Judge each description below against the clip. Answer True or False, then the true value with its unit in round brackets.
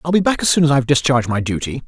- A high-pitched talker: False (140 Hz)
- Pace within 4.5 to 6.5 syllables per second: False (7.4 syllables/s)